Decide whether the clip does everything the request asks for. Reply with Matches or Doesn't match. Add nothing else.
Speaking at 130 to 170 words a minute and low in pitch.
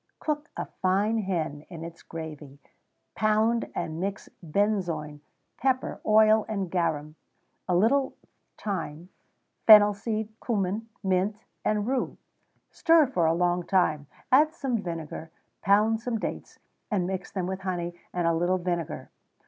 Doesn't match